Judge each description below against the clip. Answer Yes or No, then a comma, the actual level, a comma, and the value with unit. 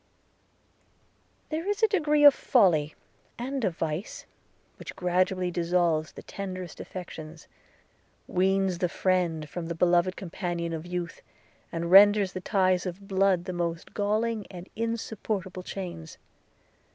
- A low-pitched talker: No, medium, 185 Hz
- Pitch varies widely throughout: No, average, 2.8 semitones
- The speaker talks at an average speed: No, slow, 125 wpm